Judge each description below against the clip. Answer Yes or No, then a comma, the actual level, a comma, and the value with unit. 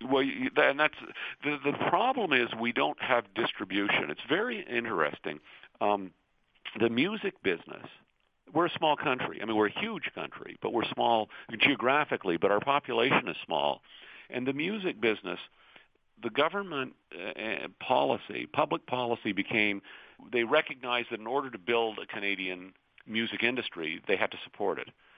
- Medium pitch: No, low, 120 Hz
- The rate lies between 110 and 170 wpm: Yes, average, 155 wpm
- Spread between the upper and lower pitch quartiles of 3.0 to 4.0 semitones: No, average, 4.8 semitones